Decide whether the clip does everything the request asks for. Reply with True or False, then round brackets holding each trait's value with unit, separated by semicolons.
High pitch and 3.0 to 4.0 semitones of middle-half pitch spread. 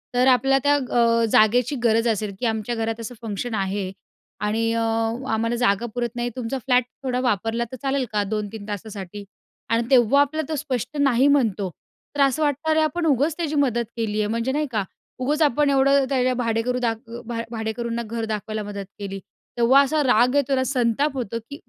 True (240 Hz; 3.5 semitones)